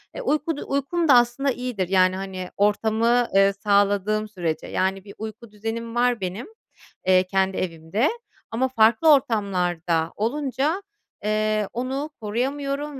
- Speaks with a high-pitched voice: Yes, high, 220 Hz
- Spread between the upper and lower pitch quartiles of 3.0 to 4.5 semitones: No, average, 5.0 semitones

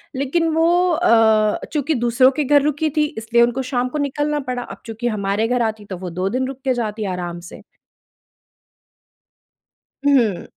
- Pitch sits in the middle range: No, high, 245 Hz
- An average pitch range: Yes, average, 4.4 semitones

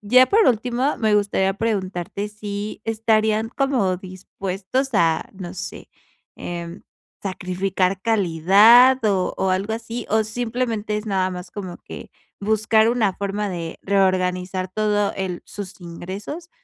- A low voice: No, high, 205 Hz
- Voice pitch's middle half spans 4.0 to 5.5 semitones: No, average, 3.0 semitones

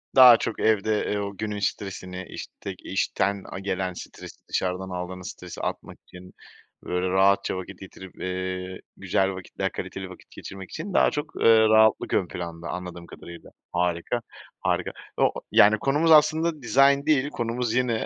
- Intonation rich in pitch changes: No, average, 4.4 semitones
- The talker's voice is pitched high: No, low, 100 Hz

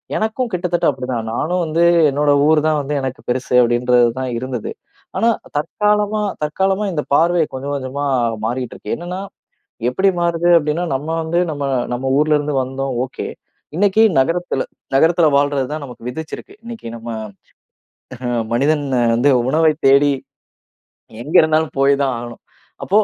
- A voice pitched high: No, medium, 150 Hz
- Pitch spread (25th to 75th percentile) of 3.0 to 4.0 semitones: No, average, 4.6 semitones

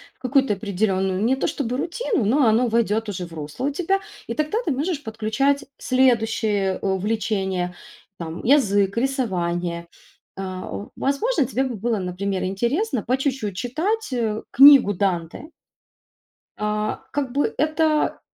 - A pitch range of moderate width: No, wide, 6.0 semitones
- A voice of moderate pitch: No, high, 225 Hz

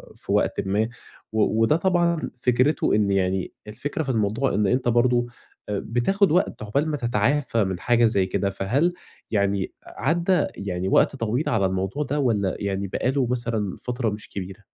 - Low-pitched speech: Yes, low, 115 Hz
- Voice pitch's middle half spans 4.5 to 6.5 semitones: Yes, average, 5.2 semitones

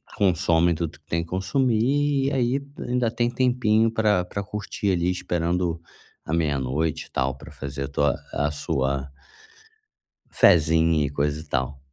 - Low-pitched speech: Yes, very low, 85 Hz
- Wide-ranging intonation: Yes, wide, 7.0 semitones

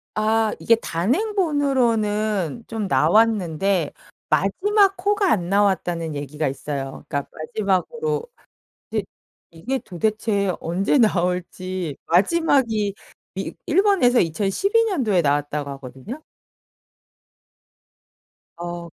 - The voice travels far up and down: Yes, wide, 6.9 semitones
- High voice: Yes, high, 200 Hz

